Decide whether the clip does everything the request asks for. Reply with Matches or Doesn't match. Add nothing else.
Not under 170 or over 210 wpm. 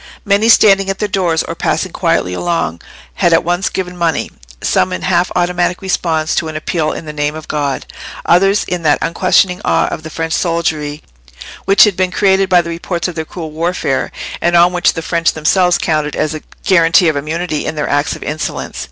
Matches